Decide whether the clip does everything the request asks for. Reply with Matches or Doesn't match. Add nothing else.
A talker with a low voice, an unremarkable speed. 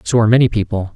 Doesn't match